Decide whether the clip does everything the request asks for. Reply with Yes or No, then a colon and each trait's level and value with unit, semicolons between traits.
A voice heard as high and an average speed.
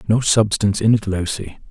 No: low, 105 Hz; average, 175 wpm